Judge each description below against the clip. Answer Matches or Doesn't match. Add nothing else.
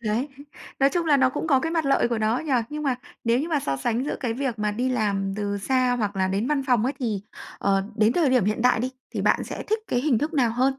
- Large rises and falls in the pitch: Doesn't match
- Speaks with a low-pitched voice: Doesn't match